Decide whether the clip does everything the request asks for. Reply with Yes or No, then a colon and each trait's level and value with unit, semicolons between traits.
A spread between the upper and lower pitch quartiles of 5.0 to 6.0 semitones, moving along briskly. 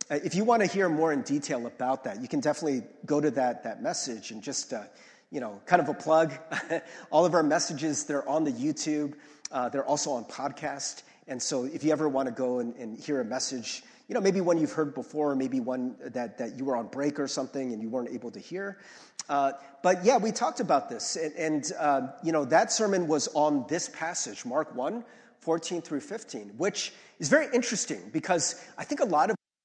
Yes: wide, 5.6 semitones; fast, 220 wpm